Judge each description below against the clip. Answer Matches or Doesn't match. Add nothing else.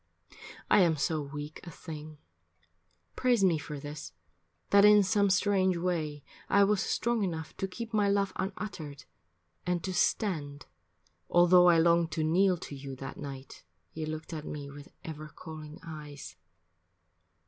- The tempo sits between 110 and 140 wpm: Doesn't match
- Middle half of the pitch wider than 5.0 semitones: Doesn't match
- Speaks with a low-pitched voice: Doesn't match